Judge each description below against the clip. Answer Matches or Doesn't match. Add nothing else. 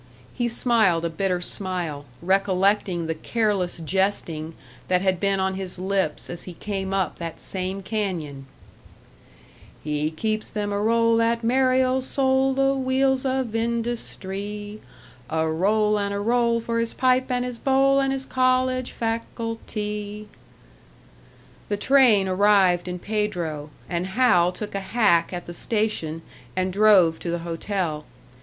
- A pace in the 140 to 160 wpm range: Matches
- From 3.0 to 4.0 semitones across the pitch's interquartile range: Doesn't match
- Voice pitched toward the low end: Doesn't match